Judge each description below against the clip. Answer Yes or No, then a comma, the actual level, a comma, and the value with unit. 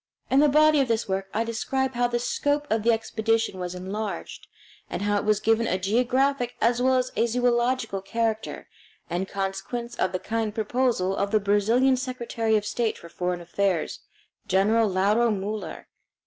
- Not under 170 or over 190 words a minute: Yes, average, 175 wpm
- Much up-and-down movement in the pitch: No, average, 3.6 semitones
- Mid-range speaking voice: No, high, 225 Hz